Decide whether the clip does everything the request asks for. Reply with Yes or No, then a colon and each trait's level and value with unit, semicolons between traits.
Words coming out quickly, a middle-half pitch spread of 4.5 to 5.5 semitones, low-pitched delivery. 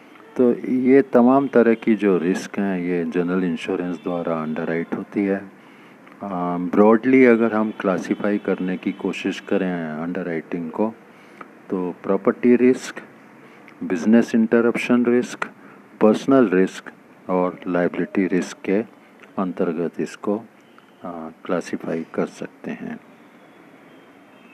No: slow, 110 wpm; average, 4.9 semitones; low, 100 Hz